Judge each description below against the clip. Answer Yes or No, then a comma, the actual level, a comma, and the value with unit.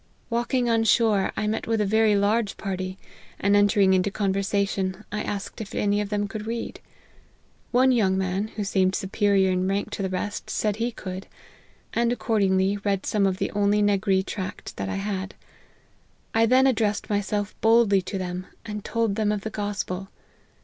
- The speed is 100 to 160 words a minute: No, average, 180 wpm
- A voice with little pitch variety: Yes, narrow, 2.2 semitones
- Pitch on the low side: No, high, 205 Hz